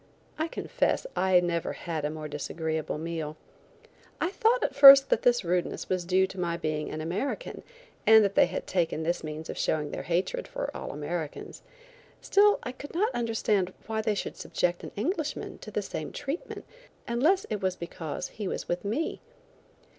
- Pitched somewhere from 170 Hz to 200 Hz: Yes, medium, 185 Hz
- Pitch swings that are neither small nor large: No, wide, 7.9 semitones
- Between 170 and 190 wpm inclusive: Yes, average, 180 wpm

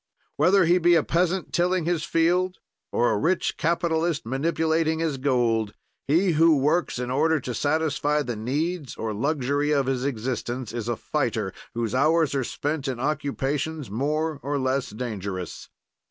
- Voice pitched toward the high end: No, medium, 145 Hz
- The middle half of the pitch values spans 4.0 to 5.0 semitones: Yes, average, 4.5 semitones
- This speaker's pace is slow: No, average, 155 wpm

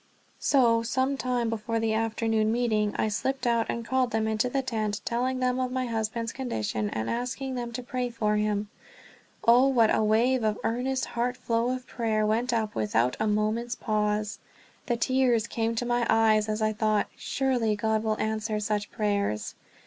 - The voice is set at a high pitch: Yes, high, 225 Hz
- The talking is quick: No, average, 180 wpm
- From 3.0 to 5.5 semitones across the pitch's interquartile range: No, narrow, 2.5 semitones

